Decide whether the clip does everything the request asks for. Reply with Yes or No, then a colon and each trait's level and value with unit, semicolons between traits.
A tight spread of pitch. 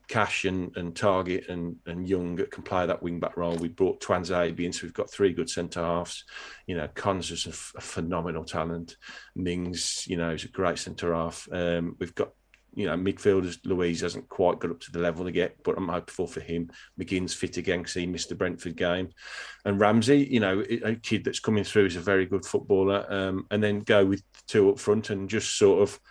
Yes: narrow, 2.3 semitones